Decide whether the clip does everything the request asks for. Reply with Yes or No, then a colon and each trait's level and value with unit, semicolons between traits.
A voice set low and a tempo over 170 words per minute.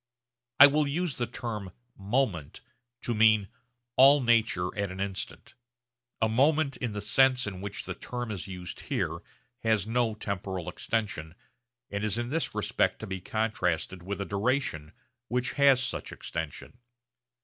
No: low, 110 Hz; average, 150 wpm